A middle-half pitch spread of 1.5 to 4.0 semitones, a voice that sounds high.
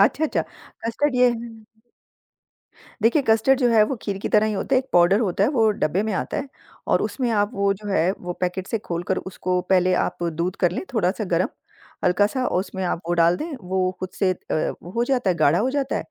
No: average, 4.4 semitones; high, 200 Hz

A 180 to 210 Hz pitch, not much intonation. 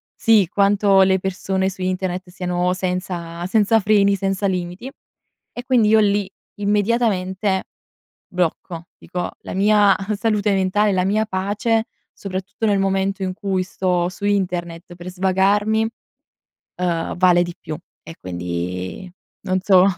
Yes: high, 190 Hz; narrow, 2.1 semitones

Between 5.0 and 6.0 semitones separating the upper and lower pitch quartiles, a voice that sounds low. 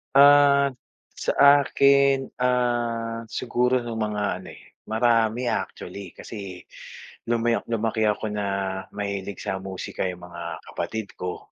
No: average, 3.7 semitones; low, 115 Hz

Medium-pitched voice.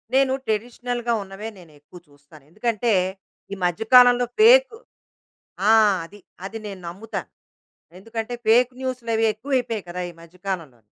No: high, 220 Hz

